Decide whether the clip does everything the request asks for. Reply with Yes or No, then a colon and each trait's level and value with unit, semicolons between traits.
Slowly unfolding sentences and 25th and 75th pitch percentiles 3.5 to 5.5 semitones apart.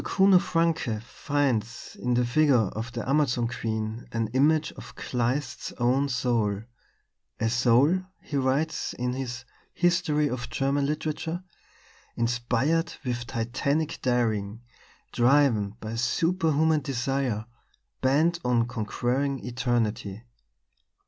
Yes: slow, 110 wpm; average, 3.8 semitones